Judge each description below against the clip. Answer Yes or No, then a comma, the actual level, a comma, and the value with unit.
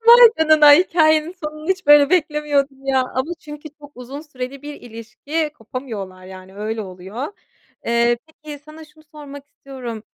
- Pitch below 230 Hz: No, very high, 285 Hz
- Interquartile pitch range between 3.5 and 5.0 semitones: Yes, average, 4.3 semitones